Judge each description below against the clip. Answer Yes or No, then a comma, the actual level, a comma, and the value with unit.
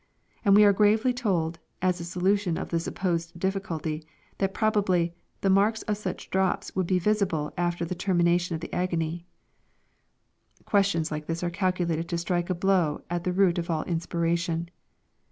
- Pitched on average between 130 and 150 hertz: No, medium, 175 Hz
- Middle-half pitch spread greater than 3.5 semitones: No, narrow, 2.4 semitones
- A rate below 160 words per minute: No, average, 175 wpm